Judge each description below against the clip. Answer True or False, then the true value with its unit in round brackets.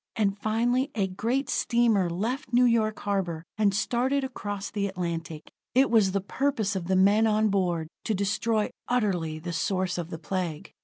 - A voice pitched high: True (200 Hz)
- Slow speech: False (170 wpm)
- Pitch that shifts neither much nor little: True (4.1 semitones)